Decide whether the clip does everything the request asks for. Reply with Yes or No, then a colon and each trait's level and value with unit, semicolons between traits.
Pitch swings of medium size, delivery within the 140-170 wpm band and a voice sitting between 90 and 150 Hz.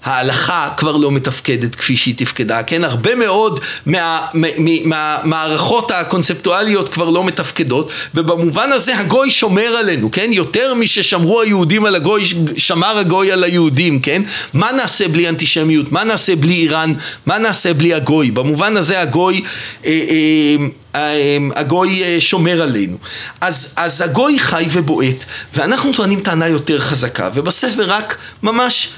No: average, 4.4 semitones; fast, 150 wpm; medium, 170 Hz